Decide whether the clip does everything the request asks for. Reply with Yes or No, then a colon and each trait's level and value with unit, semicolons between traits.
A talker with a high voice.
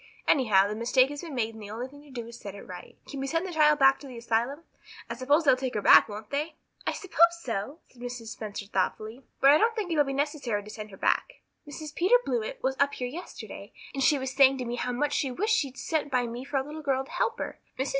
Yes: very high, 270 Hz